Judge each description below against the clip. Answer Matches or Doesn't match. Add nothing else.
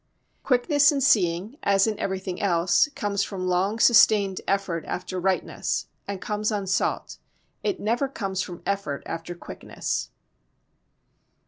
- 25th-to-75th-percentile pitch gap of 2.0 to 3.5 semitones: Matches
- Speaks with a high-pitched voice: Matches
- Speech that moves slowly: Matches